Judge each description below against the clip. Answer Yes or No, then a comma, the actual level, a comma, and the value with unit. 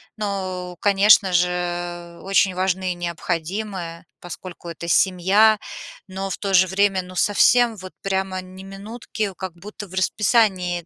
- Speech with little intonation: Yes, narrow, 2.0 semitones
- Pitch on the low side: No, medium, 185 Hz